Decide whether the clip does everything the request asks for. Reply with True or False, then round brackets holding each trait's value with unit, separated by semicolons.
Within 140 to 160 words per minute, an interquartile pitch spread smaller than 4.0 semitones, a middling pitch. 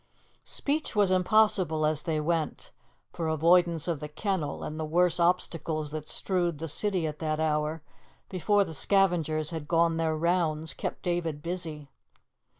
True (155 wpm; 2.5 semitones; 165 Hz)